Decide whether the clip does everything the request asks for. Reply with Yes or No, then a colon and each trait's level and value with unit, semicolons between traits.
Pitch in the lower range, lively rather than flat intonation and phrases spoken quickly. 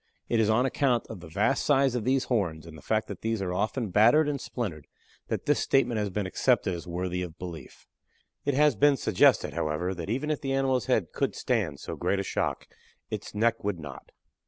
Yes: low, 110 Hz; wide, 6.5 semitones; fast, 215 wpm